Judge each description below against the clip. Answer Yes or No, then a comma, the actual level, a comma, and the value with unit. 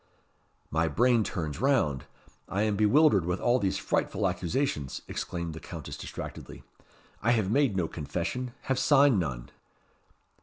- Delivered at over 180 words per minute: No, average, 140 wpm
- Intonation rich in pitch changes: Yes, wide, 7.4 semitones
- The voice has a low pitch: Yes, low, 100 Hz